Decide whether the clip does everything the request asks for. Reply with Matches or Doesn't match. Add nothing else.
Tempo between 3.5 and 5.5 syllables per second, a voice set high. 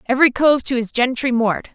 Doesn't match